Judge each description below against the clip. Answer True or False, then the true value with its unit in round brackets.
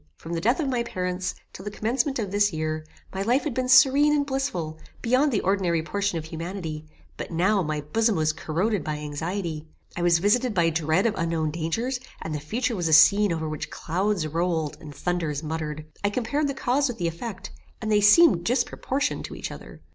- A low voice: False (185 Hz)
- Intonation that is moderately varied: False (6.5 semitones)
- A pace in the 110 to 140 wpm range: False (205 wpm)